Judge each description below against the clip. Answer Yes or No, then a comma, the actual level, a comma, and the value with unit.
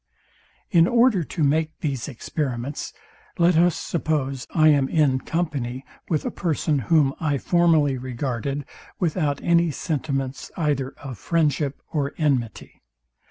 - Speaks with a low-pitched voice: No, medium, 145 Hz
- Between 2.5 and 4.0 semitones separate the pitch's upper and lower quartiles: Yes, average, 3.4 semitones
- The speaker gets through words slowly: Yes, slow, 125 wpm